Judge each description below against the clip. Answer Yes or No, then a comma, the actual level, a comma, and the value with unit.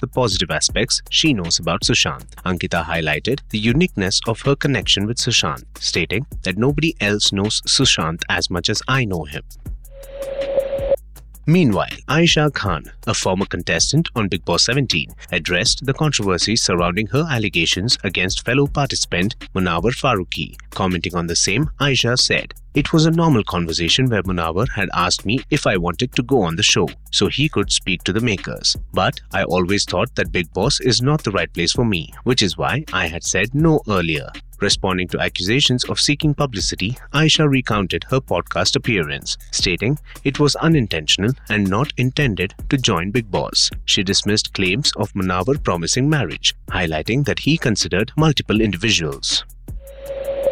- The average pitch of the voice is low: Yes, low, 110 Hz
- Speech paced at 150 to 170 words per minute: Yes, average, 165 wpm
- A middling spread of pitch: No, wide, 6.9 semitones